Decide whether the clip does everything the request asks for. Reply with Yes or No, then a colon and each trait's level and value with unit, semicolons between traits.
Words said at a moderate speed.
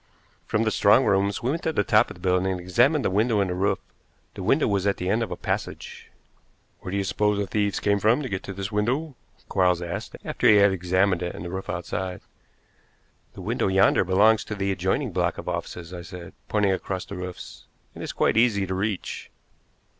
No: fast, 220 wpm